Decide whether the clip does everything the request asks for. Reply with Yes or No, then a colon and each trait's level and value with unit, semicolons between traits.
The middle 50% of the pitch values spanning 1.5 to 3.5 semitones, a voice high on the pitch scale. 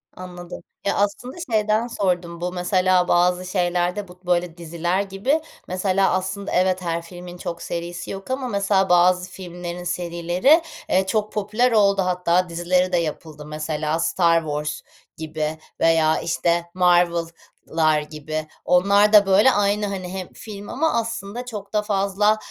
No: average, 2.8 semitones; medium, 180 Hz